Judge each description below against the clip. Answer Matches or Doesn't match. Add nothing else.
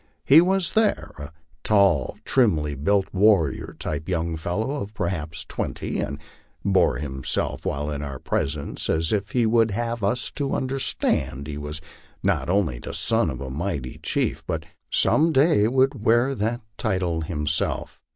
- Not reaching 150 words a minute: Doesn't match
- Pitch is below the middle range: Matches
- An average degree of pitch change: Doesn't match